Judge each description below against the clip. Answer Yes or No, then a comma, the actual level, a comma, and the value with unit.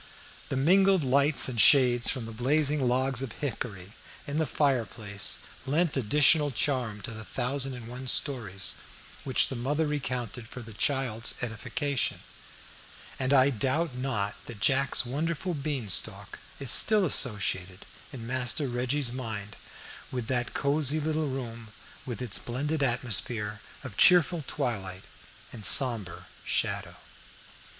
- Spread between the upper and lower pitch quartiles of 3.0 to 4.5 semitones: Yes, average, 3.9 semitones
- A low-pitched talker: Yes, low, 130 Hz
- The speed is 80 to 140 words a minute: Yes, slow, 135 wpm